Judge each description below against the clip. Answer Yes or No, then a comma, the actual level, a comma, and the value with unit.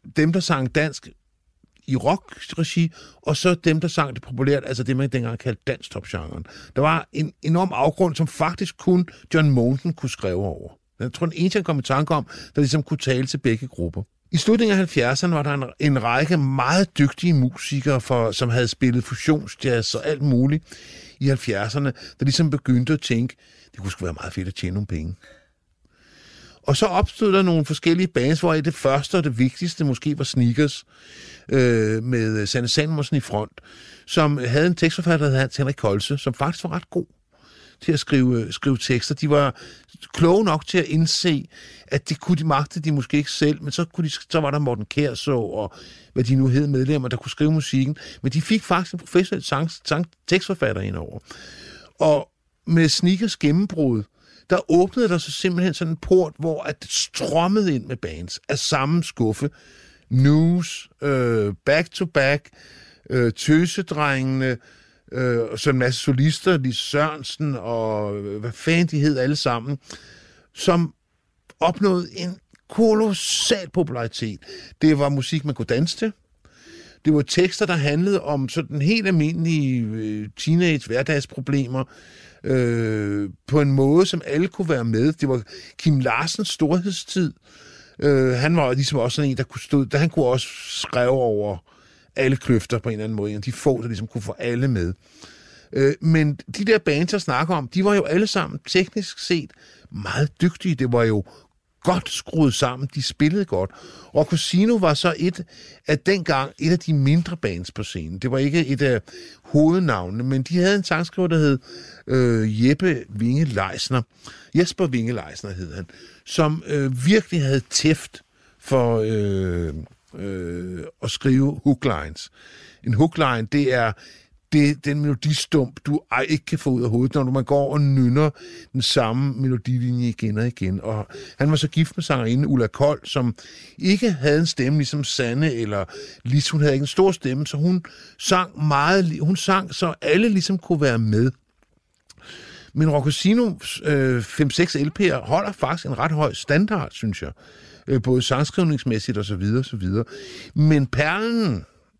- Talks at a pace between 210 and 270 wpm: No, average, 175 wpm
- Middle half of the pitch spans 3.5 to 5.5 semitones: Yes, average, 4.9 semitones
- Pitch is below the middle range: No, medium, 145 Hz